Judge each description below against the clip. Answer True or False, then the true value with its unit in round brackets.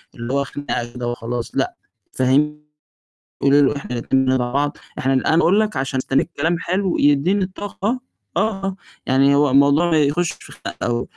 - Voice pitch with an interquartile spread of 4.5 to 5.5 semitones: True (4.9 semitones)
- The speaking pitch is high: False (140 Hz)